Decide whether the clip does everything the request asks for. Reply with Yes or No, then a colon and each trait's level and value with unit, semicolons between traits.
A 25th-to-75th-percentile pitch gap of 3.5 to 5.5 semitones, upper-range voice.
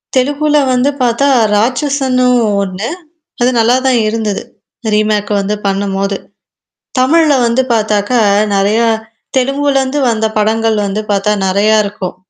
Yes: average, 4.0 semitones; high, 225 Hz